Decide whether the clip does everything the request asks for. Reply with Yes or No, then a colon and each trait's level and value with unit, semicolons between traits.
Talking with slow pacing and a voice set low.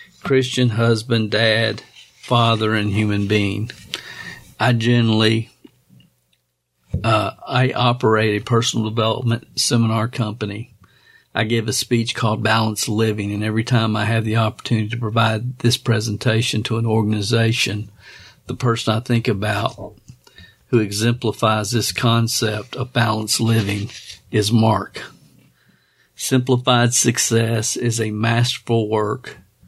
Yes: slow, 115 wpm; low, 110 Hz